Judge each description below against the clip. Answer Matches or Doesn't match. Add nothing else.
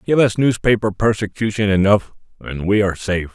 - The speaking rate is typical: Matches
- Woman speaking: Doesn't match